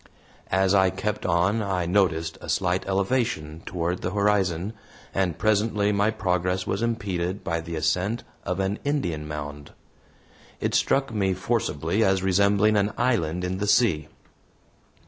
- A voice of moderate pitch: No, very low, 95 Hz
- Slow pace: No, average, 145 wpm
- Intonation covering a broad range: No, average, 3.1 semitones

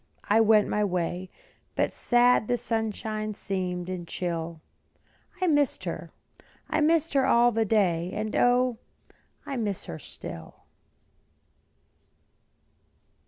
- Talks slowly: Yes, slow, 115 wpm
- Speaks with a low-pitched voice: No, high, 215 Hz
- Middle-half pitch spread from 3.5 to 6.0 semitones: Yes, average, 5.1 semitones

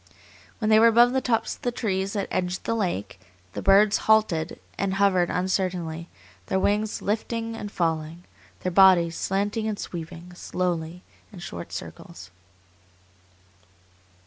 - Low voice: No, high, 190 Hz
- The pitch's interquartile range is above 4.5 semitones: No, average, 3.8 semitones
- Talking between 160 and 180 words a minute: No, average, 140 wpm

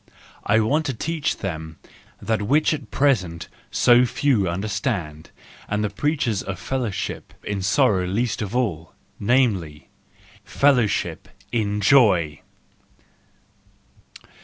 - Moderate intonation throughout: No, wide, 5.7 semitones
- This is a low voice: Yes, low, 105 Hz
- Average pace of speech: No, slow, 110 wpm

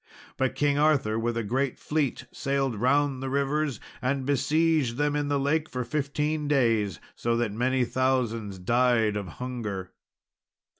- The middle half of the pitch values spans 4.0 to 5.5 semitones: No, average, 3.6 semitones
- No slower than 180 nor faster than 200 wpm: No, average, 150 wpm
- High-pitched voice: No, low, 130 Hz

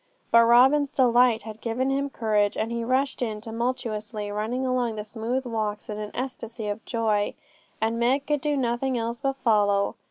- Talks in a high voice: Yes, high, 230 Hz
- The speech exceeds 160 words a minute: Yes, average, 180 wpm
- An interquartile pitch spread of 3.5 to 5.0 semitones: No, average, 3.0 semitones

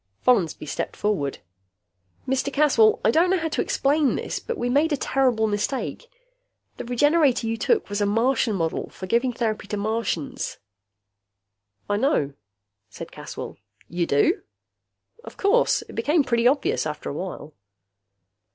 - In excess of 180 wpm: No, average, 150 wpm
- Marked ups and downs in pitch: Yes, wide, 5.8 semitones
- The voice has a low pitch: No, high, 235 Hz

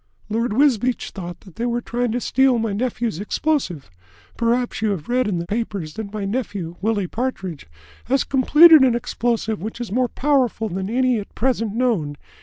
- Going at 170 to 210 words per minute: Yes, average, 180 wpm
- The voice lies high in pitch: Yes, high, 230 Hz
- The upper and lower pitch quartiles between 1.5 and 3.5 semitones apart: No, average, 4.0 semitones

